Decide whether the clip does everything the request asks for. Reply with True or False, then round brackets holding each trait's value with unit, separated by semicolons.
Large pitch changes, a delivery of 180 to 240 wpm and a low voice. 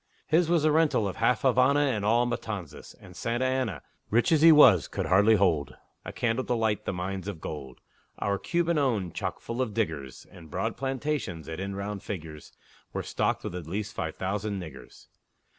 True (6.2 semitones; 190 wpm; 105 Hz)